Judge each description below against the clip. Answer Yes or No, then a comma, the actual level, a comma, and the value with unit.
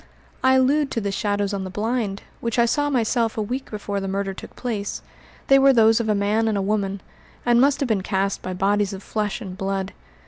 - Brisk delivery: Yes, fast, 230 wpm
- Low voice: No, high, 210 Hz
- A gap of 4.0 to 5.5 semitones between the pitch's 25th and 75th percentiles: No, average, 3.3 semitones